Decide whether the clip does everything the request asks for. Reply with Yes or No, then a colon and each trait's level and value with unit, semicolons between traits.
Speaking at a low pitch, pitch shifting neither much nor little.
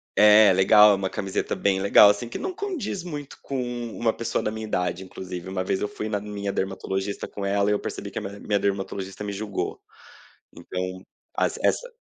No: low, 100 Hz; narrow, 2.0 semitones